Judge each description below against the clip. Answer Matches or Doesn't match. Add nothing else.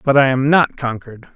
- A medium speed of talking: Doesn't match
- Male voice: Matches